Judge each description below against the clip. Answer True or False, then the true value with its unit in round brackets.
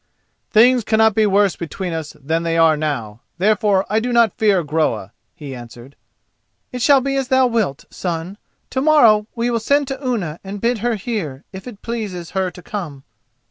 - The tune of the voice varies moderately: False (6.4 semitones)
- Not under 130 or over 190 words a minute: True (185 wpm)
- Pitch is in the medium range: False (200 Hz)